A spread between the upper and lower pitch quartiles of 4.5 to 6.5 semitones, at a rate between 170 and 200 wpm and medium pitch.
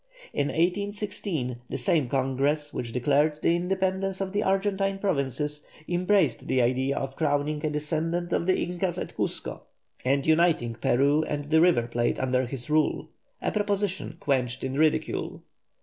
No: average, 5.3 semitones; average, 150 wpm; medium, 155 Hz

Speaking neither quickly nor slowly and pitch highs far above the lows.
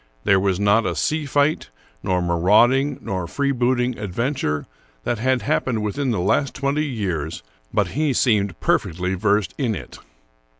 Yes: average, 145 wpm; wide, 5.9 semitones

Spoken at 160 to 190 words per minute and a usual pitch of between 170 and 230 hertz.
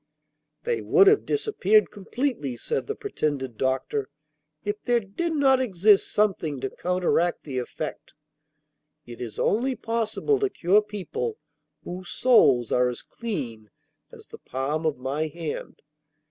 No: slow, 135 wpm; high, 190 Hz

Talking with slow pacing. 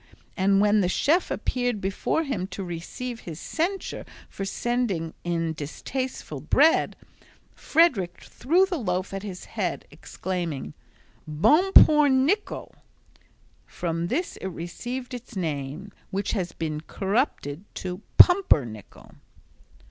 Yes: slow, 120 wpm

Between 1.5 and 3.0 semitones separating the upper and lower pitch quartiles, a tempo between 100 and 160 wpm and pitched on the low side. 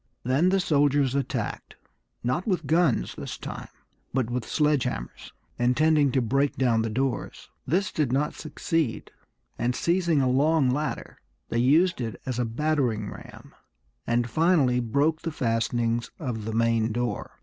No: average, 4.5 semitones; average, 150 wpm; low, 130 Hz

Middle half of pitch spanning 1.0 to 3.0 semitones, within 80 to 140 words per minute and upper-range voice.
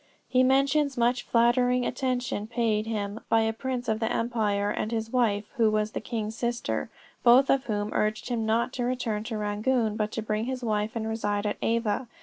No: narrow, 2.6 semitones; average, 195 wpm; high, 225 Hz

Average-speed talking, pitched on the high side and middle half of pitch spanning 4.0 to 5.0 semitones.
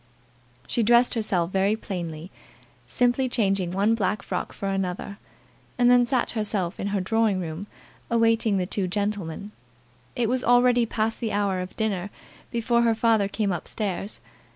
No: average, 155 wpm; high, 210 Hz; average, 3.2 semitones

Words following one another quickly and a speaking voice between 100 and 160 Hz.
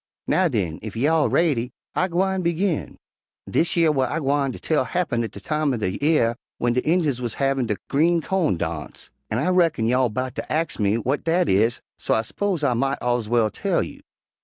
Yes: fast, 210 wpm; low, 135 Hz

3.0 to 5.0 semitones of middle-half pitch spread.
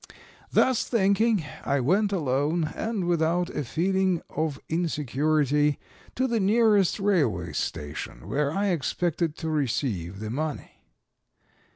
No: wide, 5.4 semitones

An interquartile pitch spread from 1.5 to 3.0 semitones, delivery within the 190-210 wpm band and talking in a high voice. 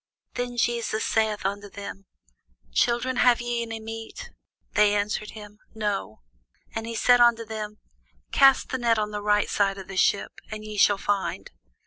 No: narrow, 2.4 semitones; average, 165 wpm; high, 215 Hz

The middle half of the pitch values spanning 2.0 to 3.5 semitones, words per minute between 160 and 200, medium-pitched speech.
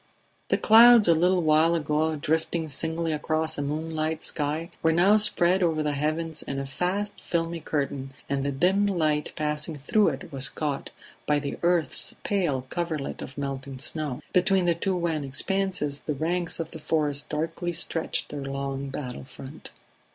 Yes: average, 3.2 semitones; average, 165 wpm; medium, 155 Hz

